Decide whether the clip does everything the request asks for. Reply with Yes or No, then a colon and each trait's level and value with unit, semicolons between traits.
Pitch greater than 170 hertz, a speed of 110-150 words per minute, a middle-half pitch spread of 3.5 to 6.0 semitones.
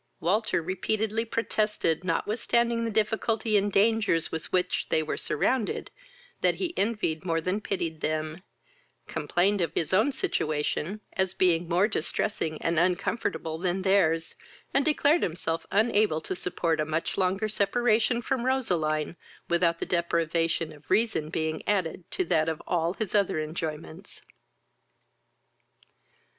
Yes: medium, 185 Hz; slow, 135 wpm; average, 4.8 semitones